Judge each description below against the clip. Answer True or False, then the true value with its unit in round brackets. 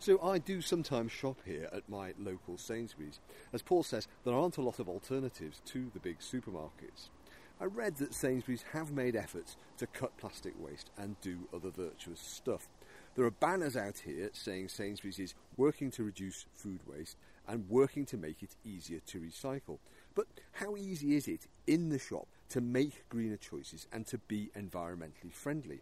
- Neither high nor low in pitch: False (115 Hz)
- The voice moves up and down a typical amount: False (6.8 semitones)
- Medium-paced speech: True (180 wpm)